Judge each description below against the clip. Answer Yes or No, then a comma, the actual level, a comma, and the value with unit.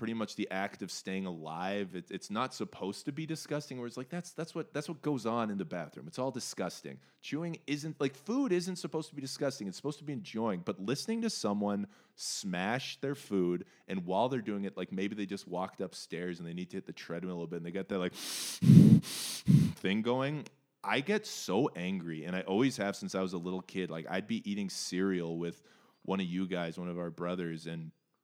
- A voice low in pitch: Yes, low, 100 Hz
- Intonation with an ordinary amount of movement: No, wide, 7.9 semitones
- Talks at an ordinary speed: No, fast, 230 wpm